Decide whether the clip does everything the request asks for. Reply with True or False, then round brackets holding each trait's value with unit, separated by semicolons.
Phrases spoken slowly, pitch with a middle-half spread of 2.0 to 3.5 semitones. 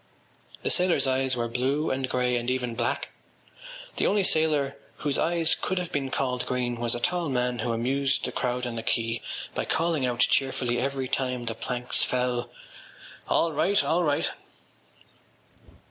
False (165 wpm; 3.0 semitones)